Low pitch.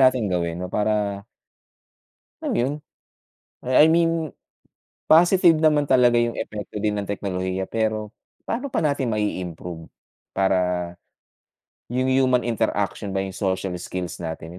Yes: low, 105 Hz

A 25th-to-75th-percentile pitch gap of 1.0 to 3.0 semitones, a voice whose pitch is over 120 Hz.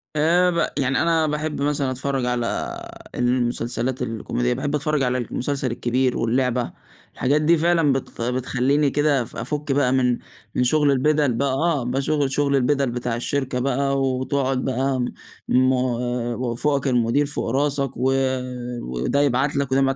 Yes: narrow, 2.5 semitones; low, 135 Hz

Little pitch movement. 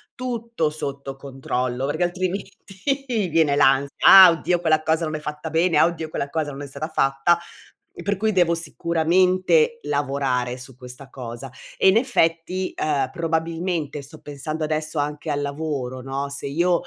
No: average, 3.5 semitones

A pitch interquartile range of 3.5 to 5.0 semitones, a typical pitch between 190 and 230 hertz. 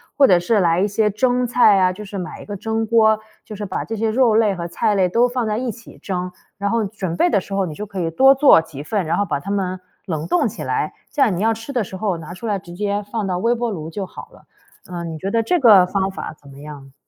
Yes: average, 3.9 semitones; high, 200 Hz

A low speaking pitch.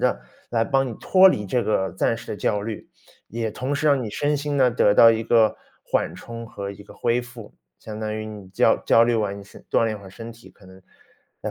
Yes: low, 115 Hz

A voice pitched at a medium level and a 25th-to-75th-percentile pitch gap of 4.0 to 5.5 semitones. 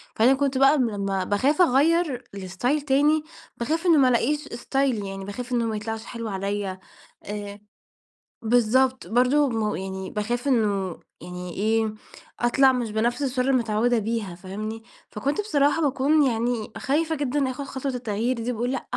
No: high, 240 Hz; average, 4.3 semitones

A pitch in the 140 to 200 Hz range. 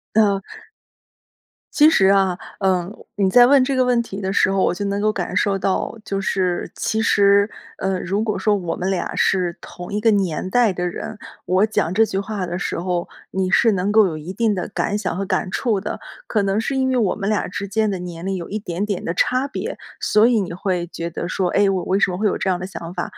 Yes: high, 195 Hz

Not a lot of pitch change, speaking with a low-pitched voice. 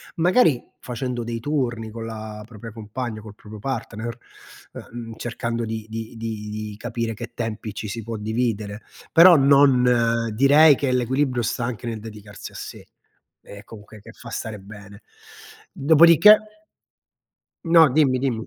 No: average, 3.3 semitones; low, 115 Hz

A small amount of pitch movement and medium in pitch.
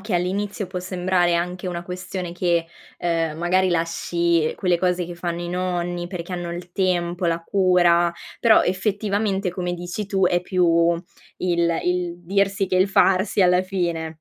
Yes: narrow, 1.3 semitones; medium, 180 Hz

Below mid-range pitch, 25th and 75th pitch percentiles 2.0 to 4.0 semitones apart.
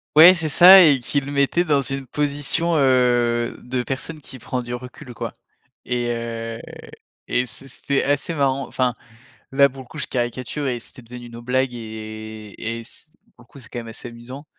Yes: low, 130 Hz; average, 2.9 semitones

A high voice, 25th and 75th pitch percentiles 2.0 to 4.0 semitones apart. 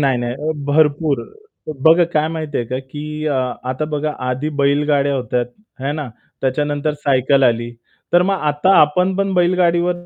No: medium, 150 Hz; average, 2.8 semitones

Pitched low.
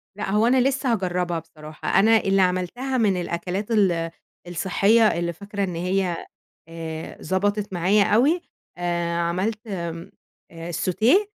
No: high, 190 Hz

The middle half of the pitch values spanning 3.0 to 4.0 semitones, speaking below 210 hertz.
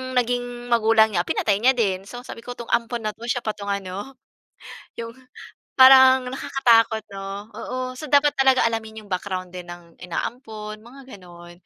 No: average, 3.7 semitones; high, 225 Hz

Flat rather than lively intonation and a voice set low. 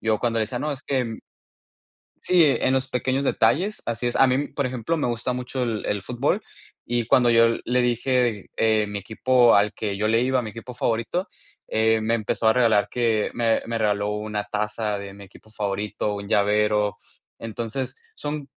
No: average, 3.0 semitones; low, 115 Hz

